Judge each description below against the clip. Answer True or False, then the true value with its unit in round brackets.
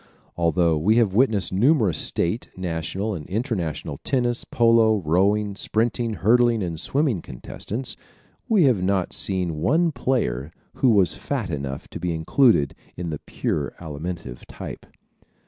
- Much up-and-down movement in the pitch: True (6.2 semitones)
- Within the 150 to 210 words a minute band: False (135 wpm)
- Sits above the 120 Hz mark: False (100 Hz)